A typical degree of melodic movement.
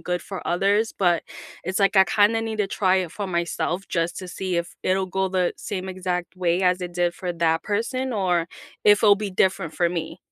No: narrow, 2.2 semitones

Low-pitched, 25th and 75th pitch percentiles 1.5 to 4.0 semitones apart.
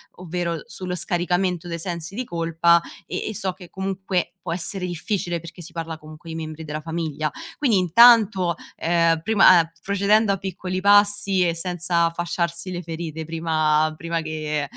No: medium, 170 Hz; narrow, 2.4 semitones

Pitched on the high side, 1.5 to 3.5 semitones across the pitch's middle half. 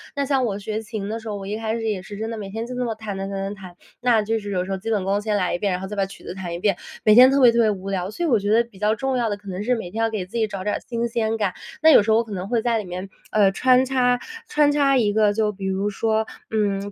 Yes: high, 215 Hz; average, 2.8 semitones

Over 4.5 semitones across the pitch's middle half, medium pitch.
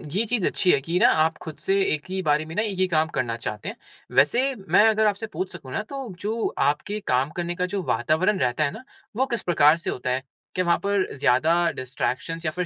Yes: wide, 5.4 semitones; medium, 175 Hz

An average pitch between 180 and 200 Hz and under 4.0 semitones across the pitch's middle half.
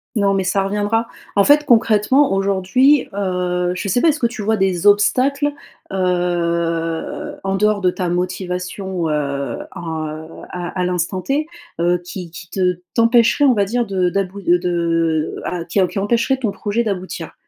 Yes: high, 190 Hz; average, 3.5 semitones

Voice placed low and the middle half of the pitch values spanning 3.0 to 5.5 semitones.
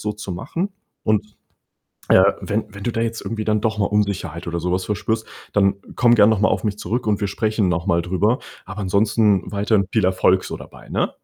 No: low, 105 Hz; narrow, 2.5 semitones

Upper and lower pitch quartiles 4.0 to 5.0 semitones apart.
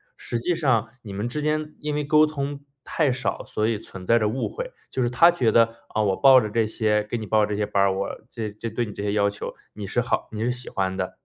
Yes: average, 4.3 semitones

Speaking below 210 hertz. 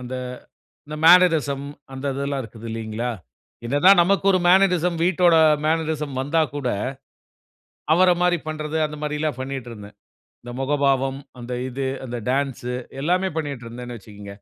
Yes: medium, 140 Hz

